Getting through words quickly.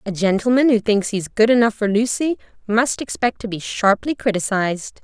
No: average, 190 wpm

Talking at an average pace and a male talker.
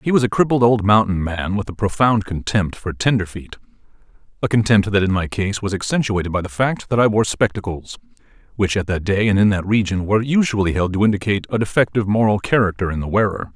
No: fast, 210 wpm; male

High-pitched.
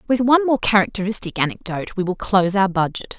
Yes: high, 200 Hz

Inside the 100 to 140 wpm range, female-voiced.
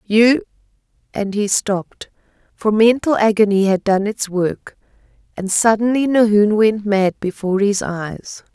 Yes: slow, 135 wpm; female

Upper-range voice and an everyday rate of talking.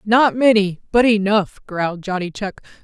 Yes: high, 205 Hz; average, 150 wpm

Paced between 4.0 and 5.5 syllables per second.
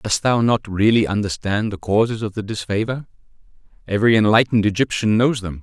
No: 5.8 syllables/s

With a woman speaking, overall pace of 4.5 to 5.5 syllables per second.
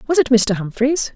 Yes: female; 5.1 syllables/s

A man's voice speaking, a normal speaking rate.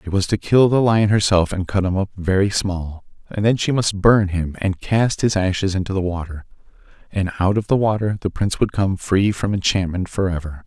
No: male; fast, 220 wpm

